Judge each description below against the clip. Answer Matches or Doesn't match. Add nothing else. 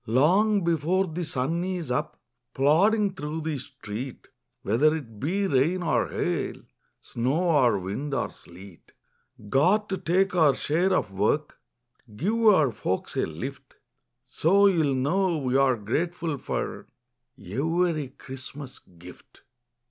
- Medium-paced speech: Doesn't match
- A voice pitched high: Doesn't match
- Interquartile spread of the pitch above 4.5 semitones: Matches